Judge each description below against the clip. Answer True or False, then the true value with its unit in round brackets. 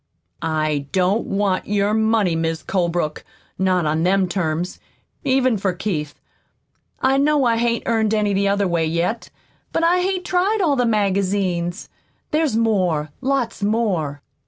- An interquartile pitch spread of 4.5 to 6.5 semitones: True (5.2 semitones)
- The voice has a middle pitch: False (200 Hz)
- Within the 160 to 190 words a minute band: False (145 wpm)